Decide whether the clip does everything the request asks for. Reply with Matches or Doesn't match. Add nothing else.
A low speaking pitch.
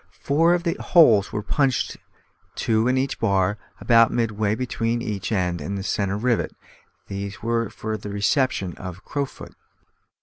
Matches